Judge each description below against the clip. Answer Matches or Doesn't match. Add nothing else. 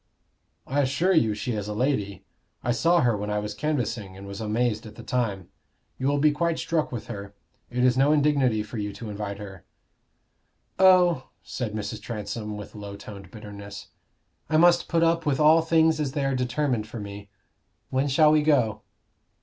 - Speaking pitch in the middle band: Doesn't match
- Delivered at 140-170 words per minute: Doesn't match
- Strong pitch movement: Matches